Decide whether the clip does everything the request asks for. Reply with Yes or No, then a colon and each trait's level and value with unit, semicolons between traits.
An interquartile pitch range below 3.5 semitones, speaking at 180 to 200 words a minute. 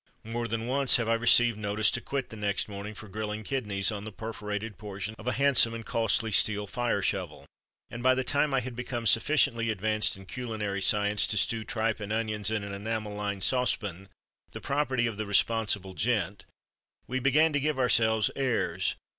Yes: average, 2.8 semitones; average, 190 wpm